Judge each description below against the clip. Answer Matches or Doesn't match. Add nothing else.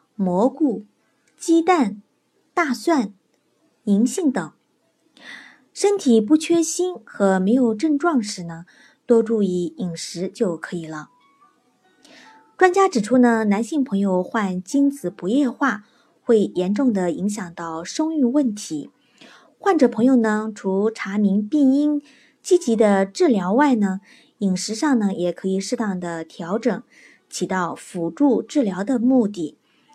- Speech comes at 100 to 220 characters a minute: Matches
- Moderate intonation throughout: Doesn't match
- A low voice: Doesn't match